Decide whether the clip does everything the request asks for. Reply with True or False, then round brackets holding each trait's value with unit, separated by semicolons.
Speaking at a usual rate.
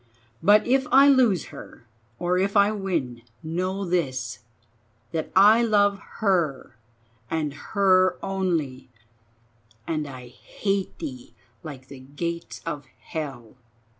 False (115 wpm)